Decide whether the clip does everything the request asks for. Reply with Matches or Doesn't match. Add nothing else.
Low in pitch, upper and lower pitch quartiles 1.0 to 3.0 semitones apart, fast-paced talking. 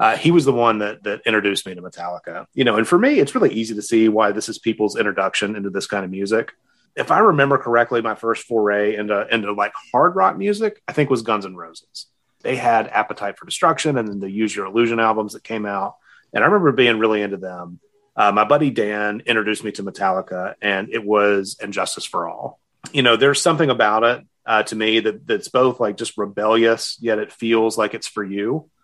Matches